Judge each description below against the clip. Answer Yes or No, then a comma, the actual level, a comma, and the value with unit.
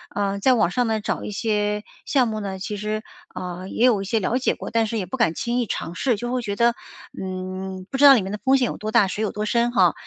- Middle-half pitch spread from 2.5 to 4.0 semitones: Yes, average, 3.4 semitones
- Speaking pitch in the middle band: No, high, 215 Hz